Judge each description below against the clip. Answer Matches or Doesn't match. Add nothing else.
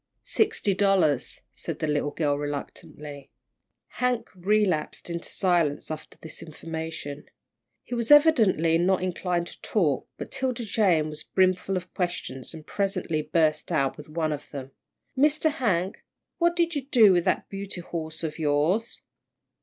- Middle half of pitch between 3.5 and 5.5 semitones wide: Matches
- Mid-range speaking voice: Matches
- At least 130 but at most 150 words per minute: Matches